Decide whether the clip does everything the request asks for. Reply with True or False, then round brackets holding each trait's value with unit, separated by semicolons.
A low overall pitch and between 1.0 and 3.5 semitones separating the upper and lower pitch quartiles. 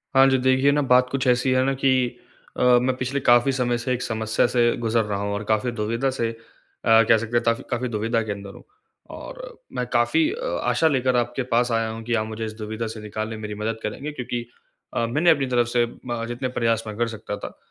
True (120 Hz; 2.5 semitones)